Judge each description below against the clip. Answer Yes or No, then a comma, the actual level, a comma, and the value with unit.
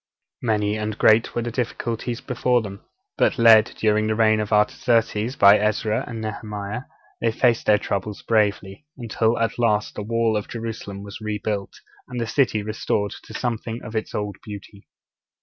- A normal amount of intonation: No, narrow, 1.8 semitones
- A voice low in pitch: Yes, low, 110 Hz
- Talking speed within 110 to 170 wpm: Yes, average, 165 wpm